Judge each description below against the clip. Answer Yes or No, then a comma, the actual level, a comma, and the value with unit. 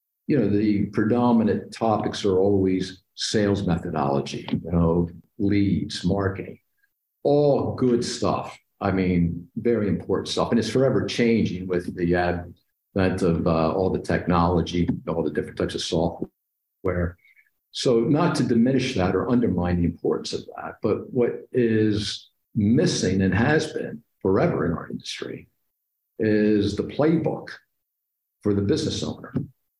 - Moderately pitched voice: No, low, 100 Hz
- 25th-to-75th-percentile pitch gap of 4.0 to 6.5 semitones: Yes, average, 4.7 semitones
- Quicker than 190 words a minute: No, slow, 135 wpm